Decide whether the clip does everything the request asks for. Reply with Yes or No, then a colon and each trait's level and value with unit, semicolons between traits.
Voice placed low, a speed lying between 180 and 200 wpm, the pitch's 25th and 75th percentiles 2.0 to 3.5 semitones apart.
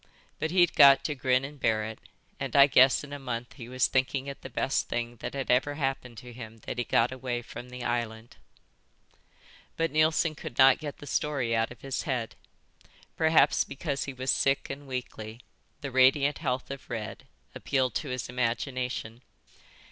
Yes: low, 130 Hz; average, 185 wpm; narrow, 2.4 semitones